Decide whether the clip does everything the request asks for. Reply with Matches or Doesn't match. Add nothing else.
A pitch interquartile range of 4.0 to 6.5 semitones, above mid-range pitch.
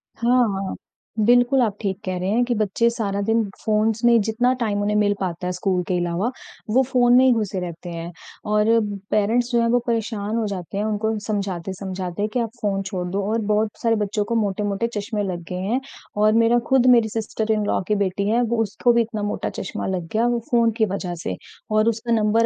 Doesn't match